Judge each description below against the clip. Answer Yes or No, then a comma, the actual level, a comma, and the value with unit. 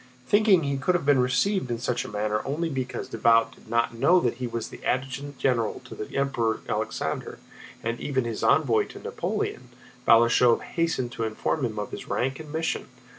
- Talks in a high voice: No, low, 125 Hz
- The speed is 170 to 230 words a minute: Yes, average, 185 wpm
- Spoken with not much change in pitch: No, average, 3.7 semitones